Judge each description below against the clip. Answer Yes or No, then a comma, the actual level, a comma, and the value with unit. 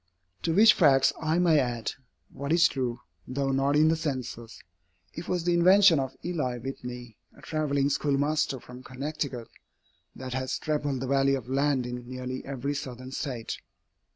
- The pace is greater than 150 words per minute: Yes, average, 160 wpm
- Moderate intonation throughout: Yes, average, 3.2 semitones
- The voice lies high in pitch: No, low, 135 Hz